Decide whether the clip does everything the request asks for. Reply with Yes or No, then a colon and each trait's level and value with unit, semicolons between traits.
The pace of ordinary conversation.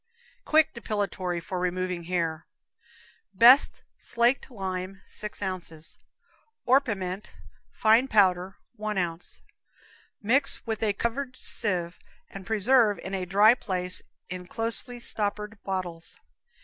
No: slow, 110 wpm